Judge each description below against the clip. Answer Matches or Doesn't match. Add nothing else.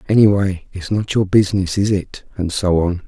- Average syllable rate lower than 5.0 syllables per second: Doesn't match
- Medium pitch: Doesn't match